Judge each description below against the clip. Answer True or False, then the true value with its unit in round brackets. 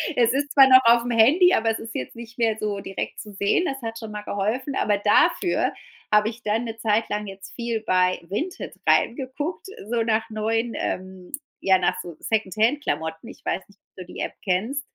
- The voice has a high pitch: True (225 Hz)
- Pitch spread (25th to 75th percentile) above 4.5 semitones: False (3.3 semitones)